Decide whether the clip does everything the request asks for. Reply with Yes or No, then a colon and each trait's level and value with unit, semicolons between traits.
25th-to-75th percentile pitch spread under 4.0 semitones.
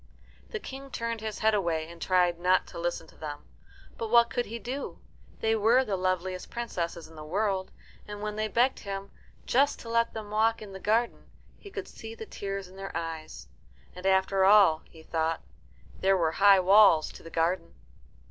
No: average, 4.4 semitones